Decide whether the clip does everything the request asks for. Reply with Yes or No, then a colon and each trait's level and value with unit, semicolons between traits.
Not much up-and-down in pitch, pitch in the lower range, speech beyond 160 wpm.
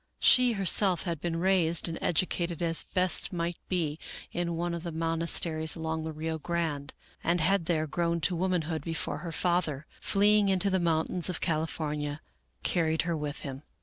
No: narrow, 2.0 semitones; medium, 170 Hz; average, 170 wpm